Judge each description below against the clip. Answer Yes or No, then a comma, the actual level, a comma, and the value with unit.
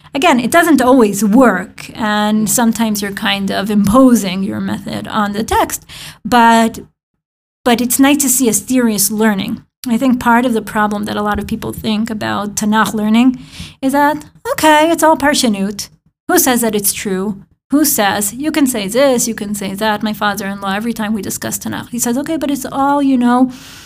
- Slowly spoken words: No, average, 190 wpm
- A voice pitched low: No, high, 230 Hz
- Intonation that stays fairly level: No, average, 3.7 semitones